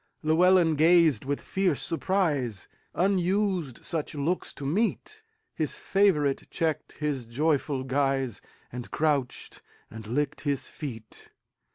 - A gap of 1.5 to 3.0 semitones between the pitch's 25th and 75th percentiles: No, average, 4.8 semitones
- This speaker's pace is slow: Yes, slow, 95 wpm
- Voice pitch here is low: No, medium, 150 Hz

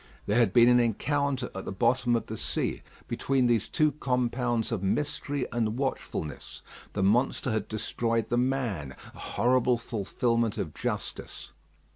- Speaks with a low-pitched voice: Yes, low, 120 Hz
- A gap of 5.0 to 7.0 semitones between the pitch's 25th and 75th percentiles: No, average, 2.7 semitones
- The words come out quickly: No, average, 150 wpm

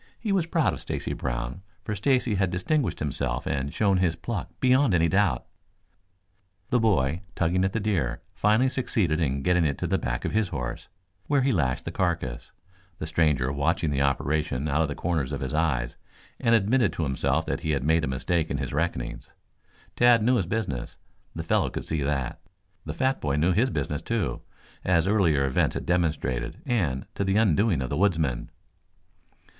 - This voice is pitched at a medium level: No, very low, 80 Hz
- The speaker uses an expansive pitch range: Yes, wide, 6.7 semitones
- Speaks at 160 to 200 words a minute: Yes, average, 190 wpm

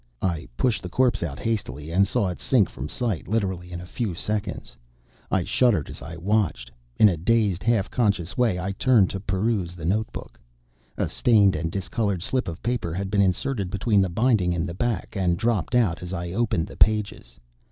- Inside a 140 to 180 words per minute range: No, average, 195 wpm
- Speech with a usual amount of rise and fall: Yes, average, 4.0 semitones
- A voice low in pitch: Yes, very low, 95 Hz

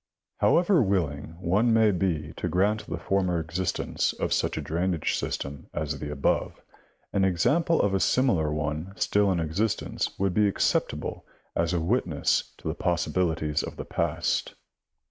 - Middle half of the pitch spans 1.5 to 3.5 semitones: No, average, 4.1 semitones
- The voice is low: Yes, very low, 90 Hz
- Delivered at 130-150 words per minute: No, average, 160 wpm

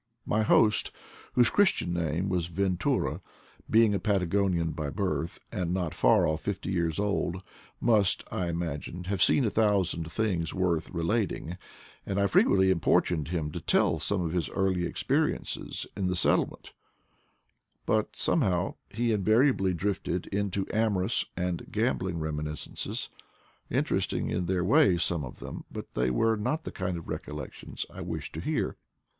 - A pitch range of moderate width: Yes, average, 3.2 semitones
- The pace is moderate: Yes, average, 155 wpm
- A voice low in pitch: Yes, very low, 90 Hz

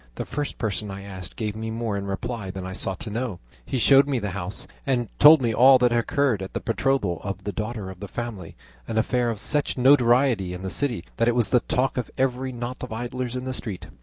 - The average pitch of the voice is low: Yes, low, 115 Hz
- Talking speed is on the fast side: Yes, fast, 245 wpm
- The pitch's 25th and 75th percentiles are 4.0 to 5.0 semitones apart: Yes, average, 4.3 semitones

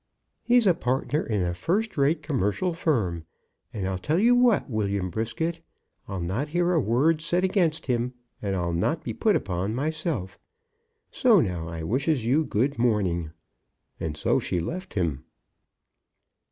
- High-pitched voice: No, low, 125 Hz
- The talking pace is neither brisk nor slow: Yes, average, 155 wpm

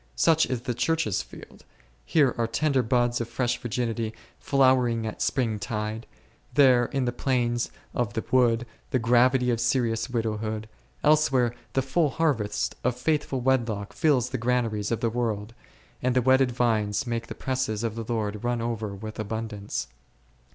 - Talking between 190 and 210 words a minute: No, average, 160 wpm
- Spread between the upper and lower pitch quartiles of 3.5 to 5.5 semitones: No, narrow, 2.6 semitones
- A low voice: Yes, low, 120 Hz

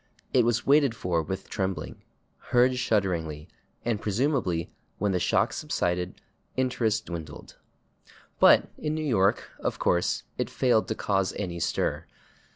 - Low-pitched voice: Yes, low, 100 Hz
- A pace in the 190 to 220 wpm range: No, slow, 135 wpm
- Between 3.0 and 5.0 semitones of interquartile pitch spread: No, wide, 5.6 semitones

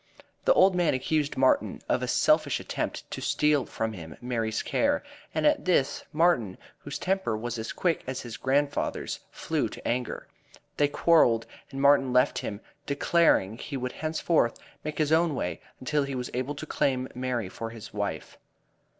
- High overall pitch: No, low, 135 Hz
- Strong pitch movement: No, average, 4.9 semitones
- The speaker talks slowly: No, average, 170 wpm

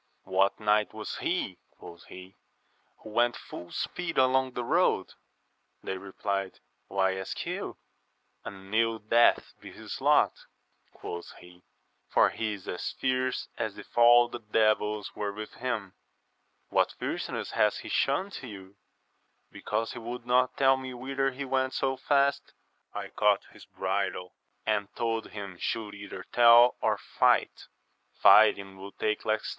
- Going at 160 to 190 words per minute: No, average, 140 wpm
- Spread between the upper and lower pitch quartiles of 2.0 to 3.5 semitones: No, average, 4.4 semitones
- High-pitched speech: No, low, 110 Hz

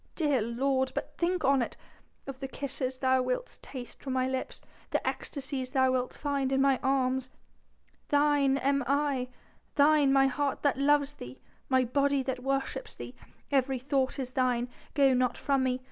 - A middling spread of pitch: No, narrow, 1.5 semitones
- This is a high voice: Yes, very high, 270 Hz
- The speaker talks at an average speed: Yes, average, 175 wpm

